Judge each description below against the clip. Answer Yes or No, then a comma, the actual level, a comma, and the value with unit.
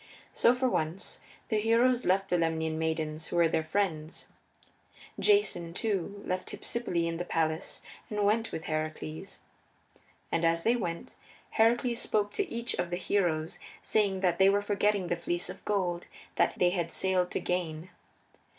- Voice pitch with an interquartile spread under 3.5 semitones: No, average, 4.0 semitones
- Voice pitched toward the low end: No, medium, 180 Hz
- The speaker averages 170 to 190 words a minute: No, average, 160 wpm